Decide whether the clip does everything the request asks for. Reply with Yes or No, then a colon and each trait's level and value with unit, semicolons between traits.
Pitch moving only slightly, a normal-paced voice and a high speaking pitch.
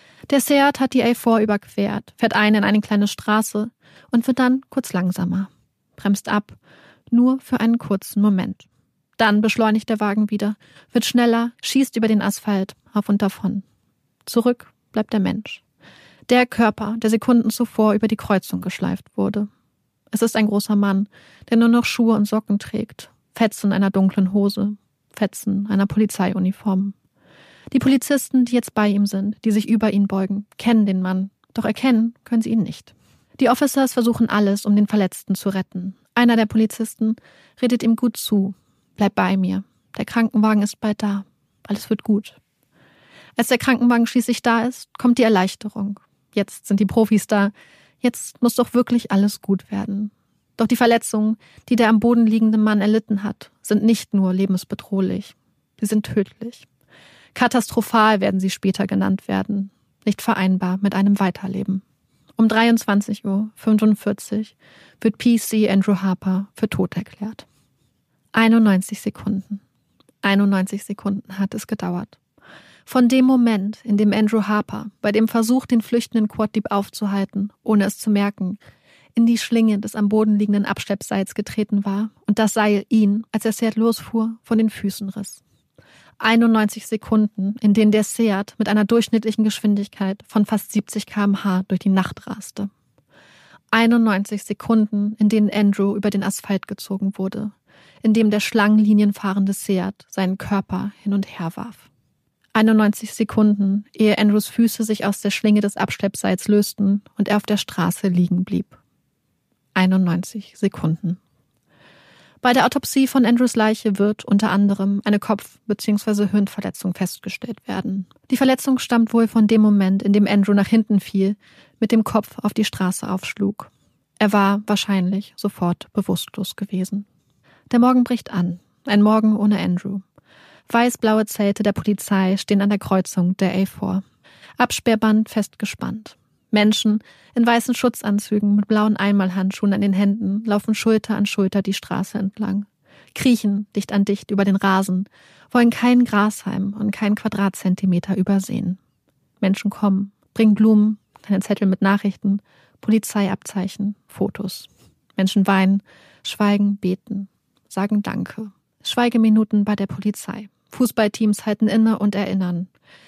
Yes: narrow, 2.0 semitones; average, 150 wpm; high, 210 Hz